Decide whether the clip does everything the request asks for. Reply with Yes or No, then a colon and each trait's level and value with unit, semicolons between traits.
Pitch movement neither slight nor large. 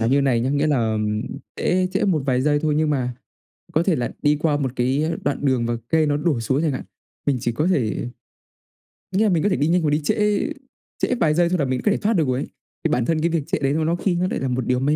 Yes: average, 4.5 semitones